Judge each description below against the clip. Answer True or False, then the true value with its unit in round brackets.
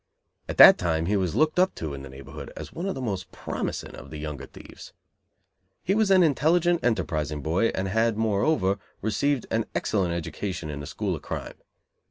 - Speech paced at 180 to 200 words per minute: True (195 wpm)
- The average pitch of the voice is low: True (100 Hz)